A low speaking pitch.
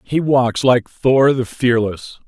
Yes: low, 125 Hz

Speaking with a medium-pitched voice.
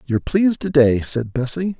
Yes: medium, 145 Hz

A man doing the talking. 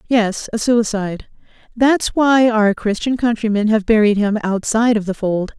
No: female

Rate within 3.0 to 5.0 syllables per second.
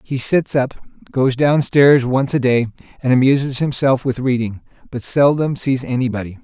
Yes: 4.7 syllables/s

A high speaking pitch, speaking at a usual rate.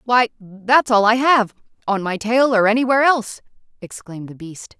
Yes: high, 225 Hz; average, 165 wpm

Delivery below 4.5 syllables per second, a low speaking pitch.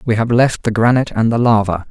No: 6.2 syllables/s; low, 115 Hz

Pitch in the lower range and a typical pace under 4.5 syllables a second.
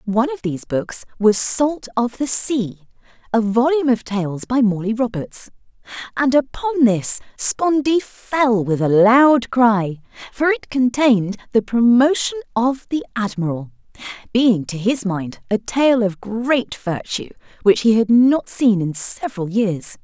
No: high, 230 Hz; 4.1 syllables/s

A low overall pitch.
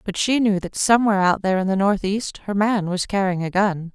No: high, 195 Hz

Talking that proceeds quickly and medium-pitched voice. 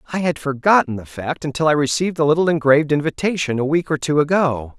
Yes: fast, 215 wpm; medium, 150 Hz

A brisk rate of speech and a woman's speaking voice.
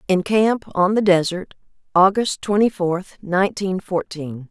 No: slow, 135 wpm; female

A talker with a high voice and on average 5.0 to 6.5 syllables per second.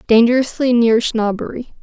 Yes: high, 235 Hz; 5.2 syllables/s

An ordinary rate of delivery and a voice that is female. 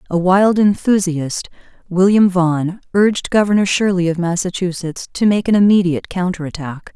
No: slow, 130 wpm; female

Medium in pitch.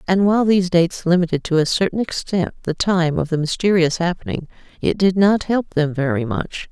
Yes: medium, 175 Hz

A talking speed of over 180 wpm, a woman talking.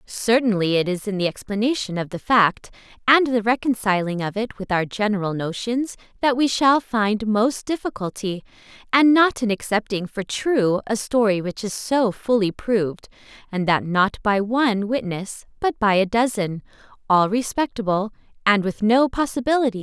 No: average, 175 wpm; female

